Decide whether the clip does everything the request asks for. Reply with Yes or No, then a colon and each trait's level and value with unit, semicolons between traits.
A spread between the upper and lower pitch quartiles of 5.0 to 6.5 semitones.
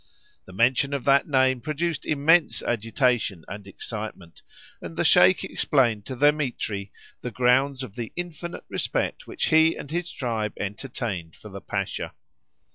Yes: average, 5.3 semitones